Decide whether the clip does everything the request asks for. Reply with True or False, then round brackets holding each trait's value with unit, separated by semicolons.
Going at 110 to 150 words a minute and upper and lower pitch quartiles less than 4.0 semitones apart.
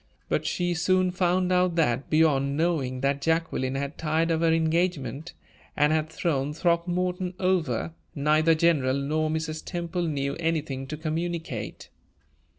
True (140 wpm; 3.1 semitones)